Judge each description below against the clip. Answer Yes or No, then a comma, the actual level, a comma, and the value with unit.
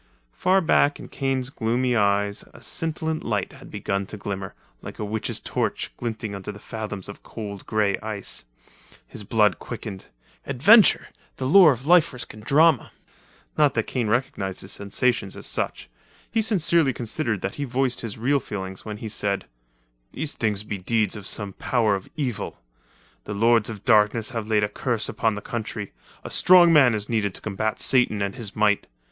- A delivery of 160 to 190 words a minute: Yes, average, 175 wpm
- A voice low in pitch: Yes, low, 110 Hz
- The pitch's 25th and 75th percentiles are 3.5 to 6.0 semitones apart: Yes, average, 4.2 semitones